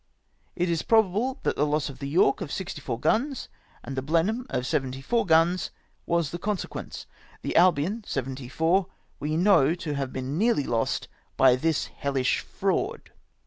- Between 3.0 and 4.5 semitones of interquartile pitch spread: No, wide, 5.6 semitones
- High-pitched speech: No, medium, 160 Hz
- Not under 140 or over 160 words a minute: Yes, average, 155 wpm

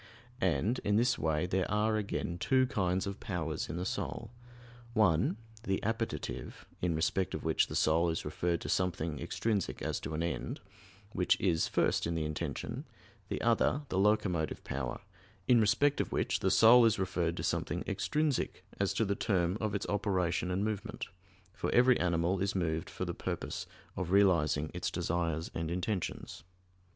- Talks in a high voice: No, very low, 95 Hz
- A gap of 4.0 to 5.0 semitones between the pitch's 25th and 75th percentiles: Yes, average, 4.3 semitones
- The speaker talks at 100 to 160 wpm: No, average, 170 wpm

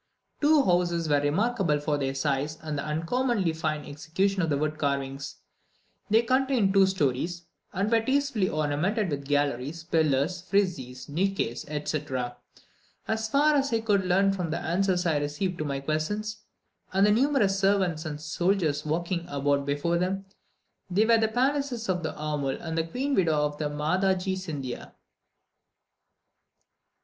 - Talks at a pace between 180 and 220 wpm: No, average, 155 wpm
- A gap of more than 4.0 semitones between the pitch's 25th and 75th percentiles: Yes, average, 5.1 semitones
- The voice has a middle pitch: Yes, medium, 170 Hz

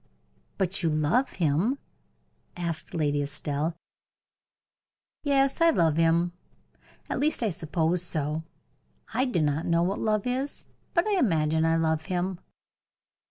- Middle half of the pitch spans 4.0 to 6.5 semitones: Yes, wide, 5.5 semitones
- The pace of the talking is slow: Yes, slow, 130 wpm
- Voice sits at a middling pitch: Yes, medium, 170 Hz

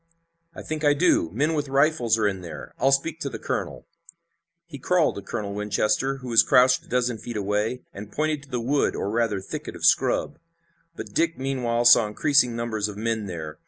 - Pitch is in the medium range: No, low, 120 Hz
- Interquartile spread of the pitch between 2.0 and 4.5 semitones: No, average, 4.9 semitones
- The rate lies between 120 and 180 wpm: No, average, 200 wpm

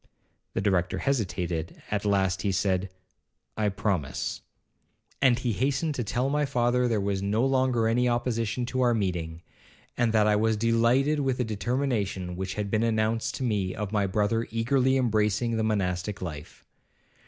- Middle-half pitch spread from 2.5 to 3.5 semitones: No, average, 3.9 semitones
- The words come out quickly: No, average, 165 wpm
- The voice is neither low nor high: No, low, 110 Hz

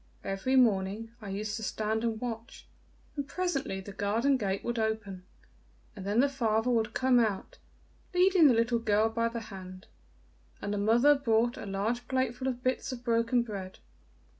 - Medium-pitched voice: No, high, 230 Hz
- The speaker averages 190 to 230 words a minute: No, average, 170 wpm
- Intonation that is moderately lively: Yes, average, 3.3 semitones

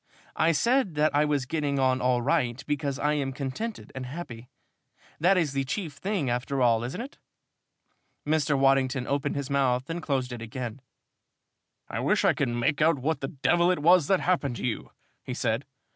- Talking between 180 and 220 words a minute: Yes, average, 190 wpm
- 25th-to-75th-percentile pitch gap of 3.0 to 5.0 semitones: Yes, average, 3.8 semitones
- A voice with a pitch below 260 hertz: Yes, medium, 140 Hz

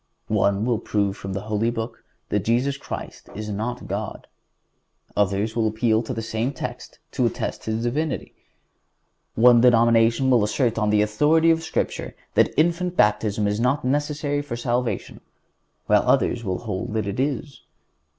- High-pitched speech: No, low, 115 Hz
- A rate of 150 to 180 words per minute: Yes, average, 160 wpm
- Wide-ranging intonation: No, average, 3.5 semitones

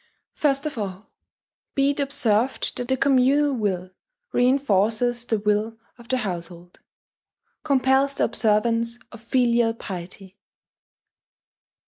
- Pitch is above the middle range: Yes, high, 235 Hz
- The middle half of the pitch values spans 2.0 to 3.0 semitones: No, average, 4.2 semitones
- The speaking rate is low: Yes, slow, 110 wpm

